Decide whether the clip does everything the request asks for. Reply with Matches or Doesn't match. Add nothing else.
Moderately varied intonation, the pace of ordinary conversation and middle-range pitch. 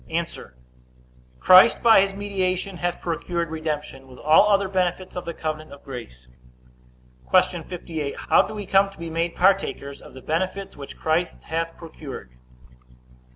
Matches